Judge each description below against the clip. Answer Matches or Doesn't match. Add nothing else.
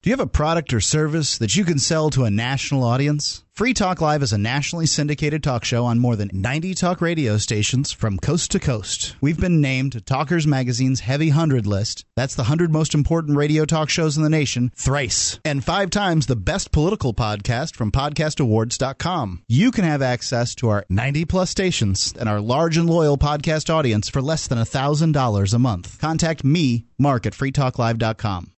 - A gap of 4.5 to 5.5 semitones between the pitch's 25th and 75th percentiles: Matches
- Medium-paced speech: Matches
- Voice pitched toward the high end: Doesn't match